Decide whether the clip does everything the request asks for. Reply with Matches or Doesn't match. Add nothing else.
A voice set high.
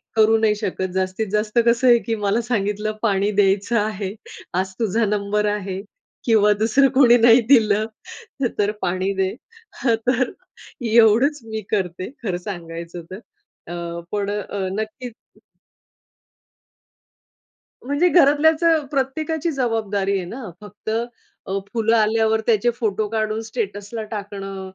Matches